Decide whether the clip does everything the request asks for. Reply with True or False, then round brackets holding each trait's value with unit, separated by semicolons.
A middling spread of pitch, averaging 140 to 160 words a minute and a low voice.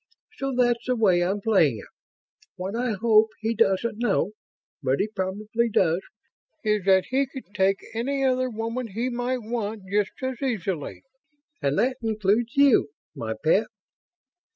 False (4.0 semitones; 155 wpm; 220 Hz)